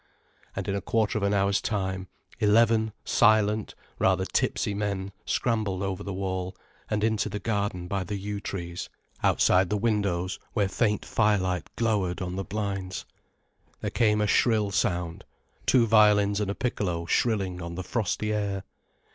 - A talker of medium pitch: No, low, 100 Hz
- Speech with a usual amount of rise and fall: No, narrow, 2.2 semitones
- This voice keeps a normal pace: Yes, average, 155 wpm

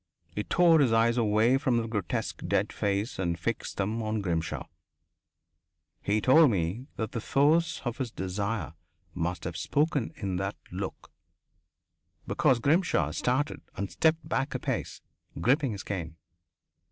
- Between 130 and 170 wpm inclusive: Yes, average, 145 wpm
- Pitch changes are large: Yes, wide, 5.7 semitones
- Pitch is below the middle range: Yes, low, 115 Hz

